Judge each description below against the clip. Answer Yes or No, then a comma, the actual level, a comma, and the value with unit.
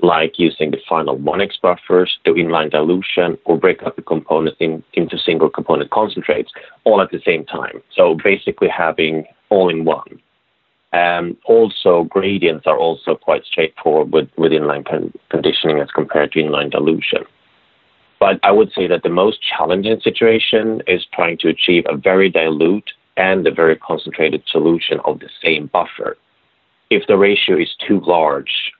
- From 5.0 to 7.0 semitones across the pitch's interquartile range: Yes, wide, 5.4 semitones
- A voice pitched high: No, very low, 90 Hz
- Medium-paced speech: Yes, average, 165 wpm